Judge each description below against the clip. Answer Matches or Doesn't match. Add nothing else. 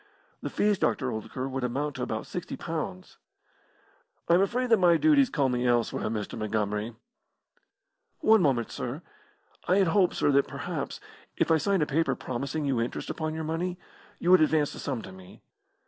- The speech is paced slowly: Doesn't match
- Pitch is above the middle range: Doesn't match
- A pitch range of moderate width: Doesn't match